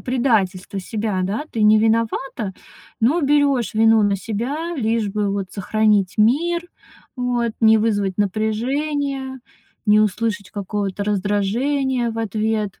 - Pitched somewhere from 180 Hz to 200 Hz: No, high, 220 Hz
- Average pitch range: Yes, average, 3.5 semitones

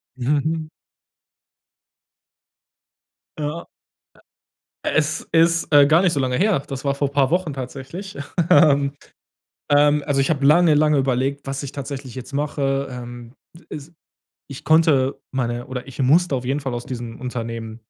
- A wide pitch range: No, average, 2.8 semitones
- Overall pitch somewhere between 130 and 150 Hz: Yes, medium, 140 Hz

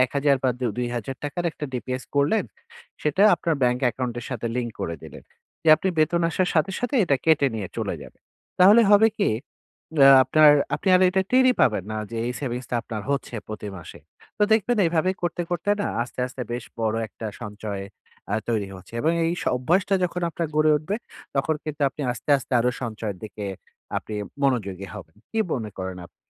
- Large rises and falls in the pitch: Yes, wide, 6.5 semitones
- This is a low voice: Yes, low, 130 Hz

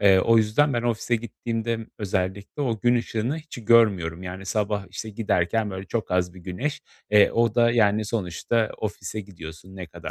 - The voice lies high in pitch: No, low, 105 Hz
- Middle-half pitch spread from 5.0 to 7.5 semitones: No, average, 3.7 semitones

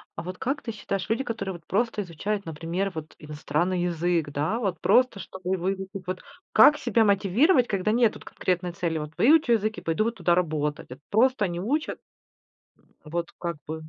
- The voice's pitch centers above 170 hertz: Yes, high, 190 Hz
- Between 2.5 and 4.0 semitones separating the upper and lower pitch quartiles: No, average, 4.7 semitones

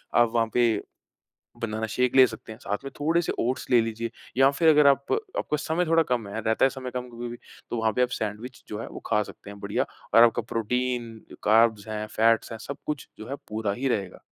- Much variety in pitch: No, average, 3.0 semitones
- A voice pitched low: Yes, low, 120 Hz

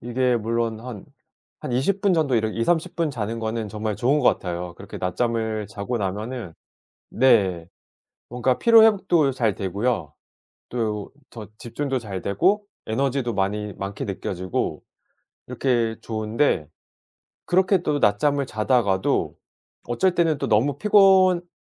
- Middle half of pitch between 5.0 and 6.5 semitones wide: Yes, average, 5.3 semitones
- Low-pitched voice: Yes, low, 115 Hz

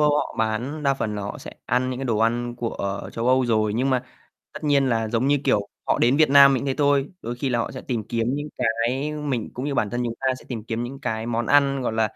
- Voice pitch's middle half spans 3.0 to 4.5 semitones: Yes, average, 3.3 semitones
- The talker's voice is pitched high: No, low, 125 Hz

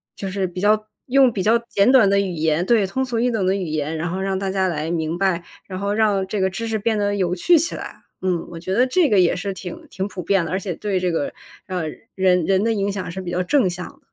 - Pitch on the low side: No, high, 190 Hz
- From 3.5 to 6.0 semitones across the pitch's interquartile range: No, average, 2.7 semitones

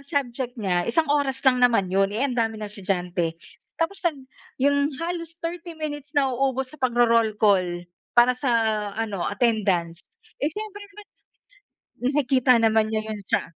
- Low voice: No, high, 245 Hz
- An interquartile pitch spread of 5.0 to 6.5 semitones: Yes, wide, 5.5 semitones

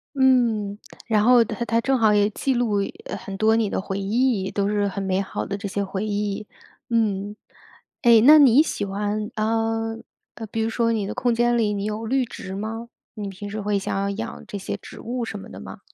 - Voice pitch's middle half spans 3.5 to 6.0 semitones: No, narrow, 2.4 semitones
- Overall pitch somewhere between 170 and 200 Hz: No, high, 215 Hz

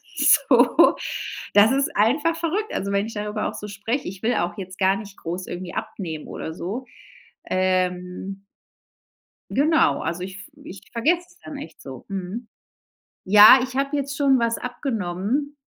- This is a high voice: Yes, high, 210 Hz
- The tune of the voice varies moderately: No, wide, 6.6 semitones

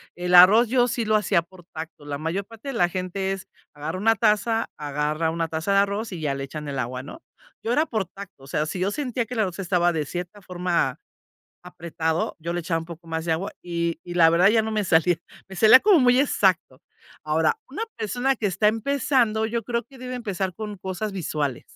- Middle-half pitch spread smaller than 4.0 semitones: No, average, 5.1 semitones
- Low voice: No, medium, 185 Hz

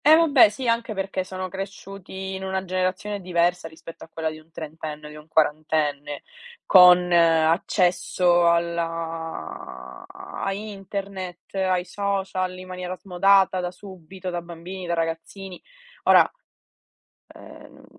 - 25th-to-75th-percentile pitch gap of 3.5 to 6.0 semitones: No, average, 2.7 semitones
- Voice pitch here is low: No, medium, 180 Hz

